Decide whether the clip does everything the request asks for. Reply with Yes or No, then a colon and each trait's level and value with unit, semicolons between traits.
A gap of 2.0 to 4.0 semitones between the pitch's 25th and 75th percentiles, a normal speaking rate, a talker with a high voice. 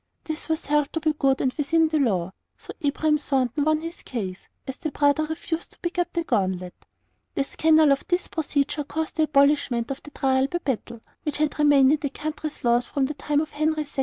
No: narrow, 2.6 semitones; fast, 220 wpm; very high, 295 Hz